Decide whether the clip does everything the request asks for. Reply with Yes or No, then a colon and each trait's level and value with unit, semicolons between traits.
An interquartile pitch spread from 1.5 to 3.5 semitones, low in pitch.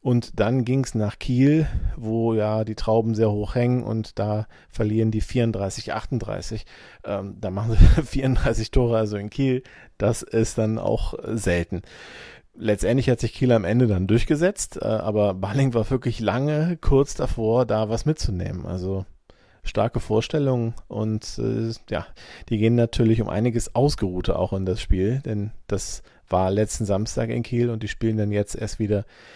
Yes: average, 2.9 semitones; low, 110 Hz